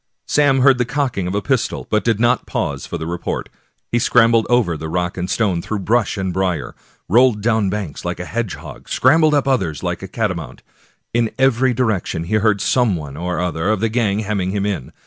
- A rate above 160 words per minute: Yes, fast, 205 wpm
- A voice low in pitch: Yes, low, 105 Hz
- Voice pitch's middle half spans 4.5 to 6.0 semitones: Yes, average, 5.2 semitones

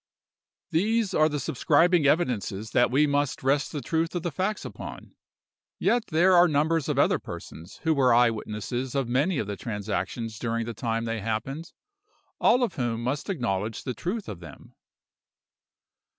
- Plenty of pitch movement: Yes, wide, 6.2 semitones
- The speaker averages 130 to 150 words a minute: No, average, 165 wpm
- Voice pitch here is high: No, low, 135 Hz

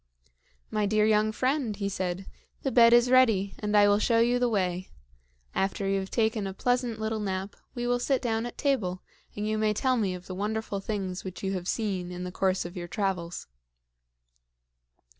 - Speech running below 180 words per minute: No, average, 195 wpm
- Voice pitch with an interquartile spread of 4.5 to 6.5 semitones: No, average, 3.3 semitones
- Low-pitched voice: No, high, 210 Hz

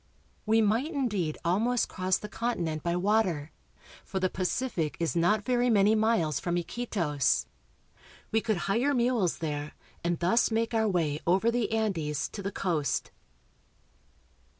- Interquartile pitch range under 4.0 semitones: No, average, 4.9 semitones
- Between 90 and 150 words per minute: Yes, average, 145 wpm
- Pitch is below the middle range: No, high, 195 Hz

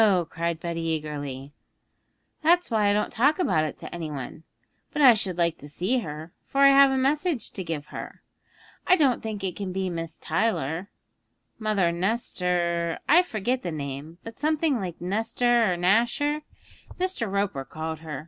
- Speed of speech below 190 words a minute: Yes, average, 170 wpm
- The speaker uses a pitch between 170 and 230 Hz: Yes, high, 190 Hz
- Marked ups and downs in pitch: Yes, wide, 6.8 semitones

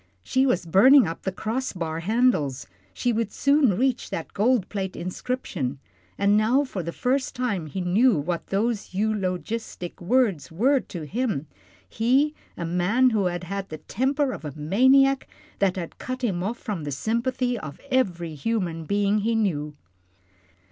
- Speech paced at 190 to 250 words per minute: No, average, 165 wpm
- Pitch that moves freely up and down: Yes, wide, 6.3 semitones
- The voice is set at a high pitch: Yes, high, 205 Hz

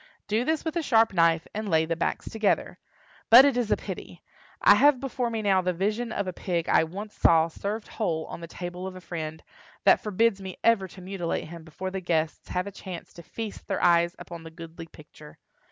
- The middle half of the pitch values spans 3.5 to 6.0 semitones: Yes, average, 4.5 semitones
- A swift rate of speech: Yes, fast, 220 wpm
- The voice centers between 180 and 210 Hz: Yes, medium, 185 Hz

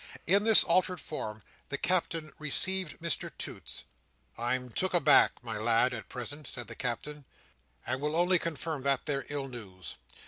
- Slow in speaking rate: No, average, 160 wpm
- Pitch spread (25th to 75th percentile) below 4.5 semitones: No, wide, 5.4 semitones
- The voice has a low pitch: No, medium, 145 Hz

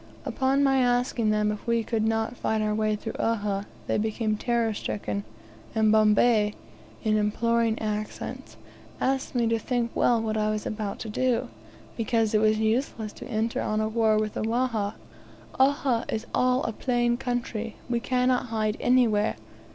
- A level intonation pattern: Yes, narrow, 2.1 semitones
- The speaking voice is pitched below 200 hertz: No, high, 225 Hz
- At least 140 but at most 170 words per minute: Yes, average, 165 wpm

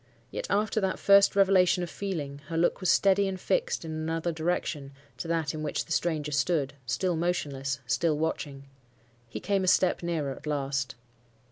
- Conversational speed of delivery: Yes, average, 165 wpm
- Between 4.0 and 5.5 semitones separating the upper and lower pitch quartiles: Yes, average, 4.5 semitones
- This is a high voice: No, medium, 165 Hz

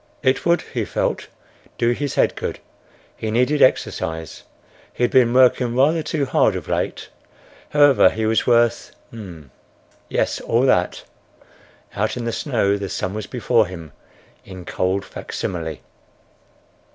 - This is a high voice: No, low, 115 Hz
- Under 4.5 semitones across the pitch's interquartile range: No, wide, 5.5 semitones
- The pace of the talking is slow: Yes, slow, 130 wpm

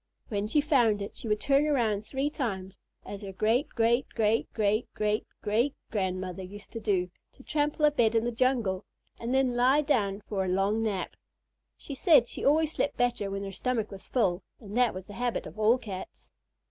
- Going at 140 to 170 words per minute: No, average, 200 wpm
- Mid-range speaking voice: No, high, 225 Hz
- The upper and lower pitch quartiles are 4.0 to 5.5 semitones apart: Yes, average, 4.3 semitones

